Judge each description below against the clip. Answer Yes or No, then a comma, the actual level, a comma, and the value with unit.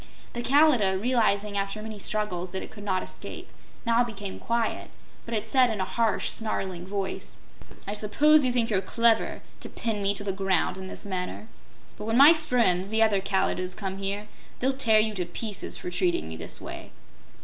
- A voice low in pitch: No, high, 210 Hz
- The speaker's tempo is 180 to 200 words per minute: Yes, average, 195 wpm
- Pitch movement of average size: Yes, average, 3.4 semitones